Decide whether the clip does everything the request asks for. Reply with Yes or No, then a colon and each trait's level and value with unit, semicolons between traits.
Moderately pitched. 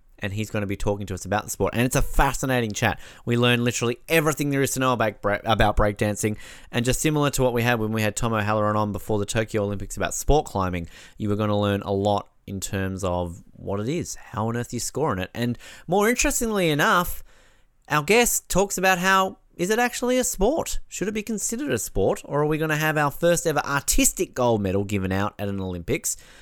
No: low, 120 Hz